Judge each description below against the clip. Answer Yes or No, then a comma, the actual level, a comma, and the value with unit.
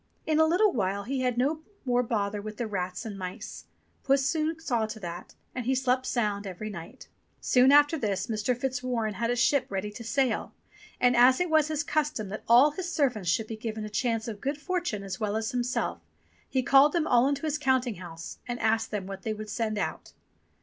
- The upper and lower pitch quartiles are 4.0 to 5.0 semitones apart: Yes, average, 4.5 semitones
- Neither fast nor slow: No, fast, 215 wpm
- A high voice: Yes, high, 240 Hz